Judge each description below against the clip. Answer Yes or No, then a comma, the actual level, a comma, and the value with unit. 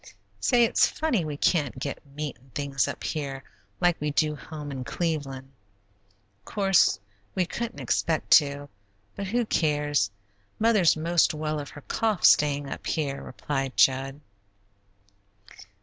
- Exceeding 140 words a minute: No, slow, 135 wpm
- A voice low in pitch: No, medium, 150 Hz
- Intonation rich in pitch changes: No, average, 3.7 semitones